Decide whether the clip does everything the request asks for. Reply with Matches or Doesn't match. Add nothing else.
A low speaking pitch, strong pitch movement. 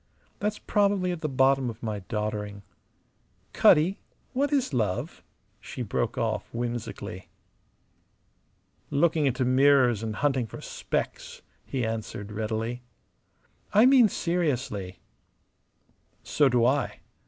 Matches